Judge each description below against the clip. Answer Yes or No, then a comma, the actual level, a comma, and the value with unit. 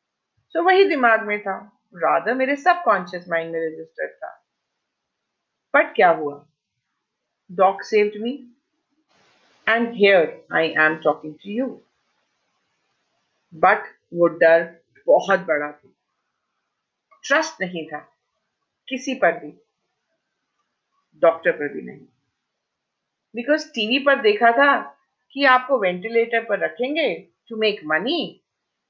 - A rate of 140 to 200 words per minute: No, slow, 110 wpm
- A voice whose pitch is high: Yes, high, 210 Hz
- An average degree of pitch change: No, wide, 7.7 semitones